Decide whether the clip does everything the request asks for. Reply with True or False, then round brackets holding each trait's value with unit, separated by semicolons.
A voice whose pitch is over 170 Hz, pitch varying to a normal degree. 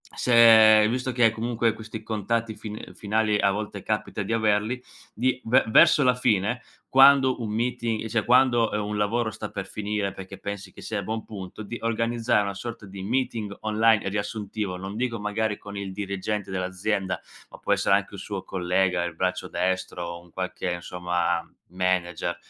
False (105 Hz; 3.0 semitones)